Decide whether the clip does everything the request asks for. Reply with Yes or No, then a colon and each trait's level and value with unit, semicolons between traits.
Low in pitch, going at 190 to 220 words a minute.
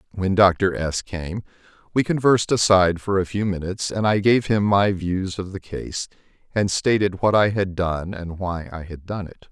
Yes: very low, 95 Hz; average, 200 wpm